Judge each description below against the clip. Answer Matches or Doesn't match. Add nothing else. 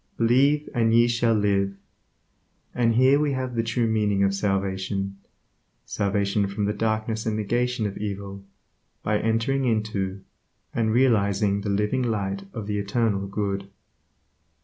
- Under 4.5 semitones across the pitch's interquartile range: Matches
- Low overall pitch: Matches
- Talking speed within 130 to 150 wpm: Matches